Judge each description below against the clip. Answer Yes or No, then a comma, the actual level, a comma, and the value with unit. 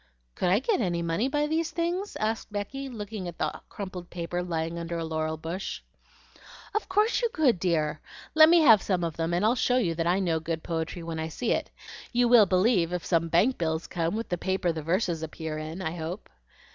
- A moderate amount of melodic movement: No, wide, 5.9 semitones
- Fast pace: Yes, fast, 220 wpm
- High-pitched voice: No, medium, 180 Hz